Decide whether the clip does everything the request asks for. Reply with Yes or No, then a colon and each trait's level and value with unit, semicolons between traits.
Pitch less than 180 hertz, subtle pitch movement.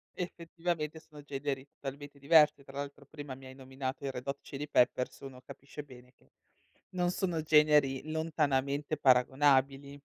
Yes: medium, 140 Hz; narrow, 2.2 semitones